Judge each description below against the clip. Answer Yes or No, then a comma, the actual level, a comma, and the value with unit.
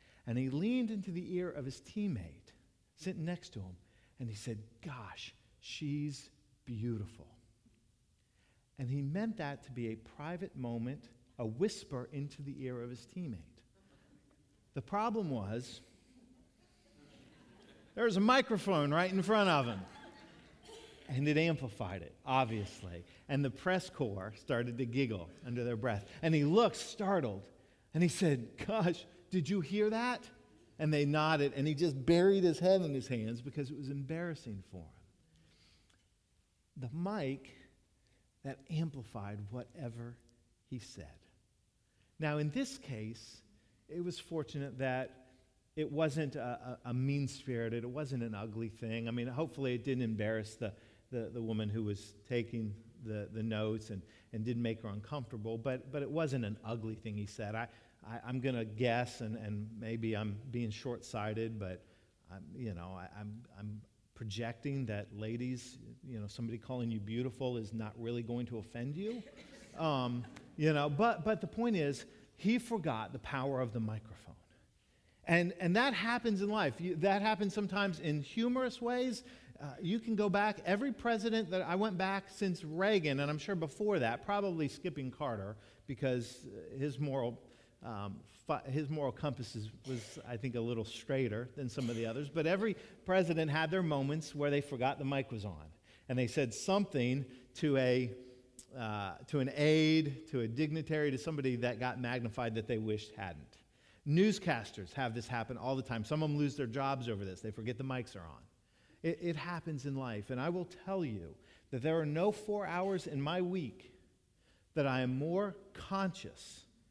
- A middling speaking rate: Yes, average, 170 wpm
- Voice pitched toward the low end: Yes, low, 130 Hz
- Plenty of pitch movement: Yes, wide, 6.1 semitones